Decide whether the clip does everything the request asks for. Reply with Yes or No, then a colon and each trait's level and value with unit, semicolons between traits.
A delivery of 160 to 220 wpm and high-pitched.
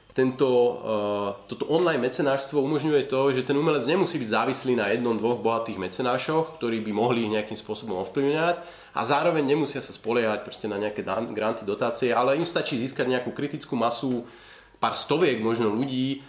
No: fast, 165 wpm; low, 125 Hz